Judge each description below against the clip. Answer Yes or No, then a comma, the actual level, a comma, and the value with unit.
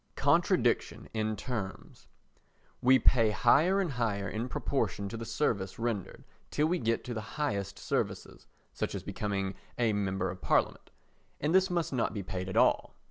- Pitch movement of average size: Yes, average, 4.7 semitones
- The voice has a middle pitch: No, low, 115 Hz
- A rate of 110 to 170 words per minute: Yes, average, 165 wpm